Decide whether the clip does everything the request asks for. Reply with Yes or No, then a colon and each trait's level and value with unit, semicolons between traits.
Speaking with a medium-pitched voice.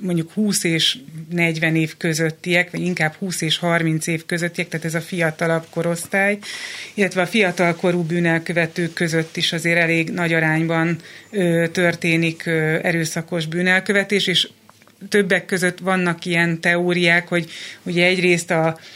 Yes: medium, 170 Hz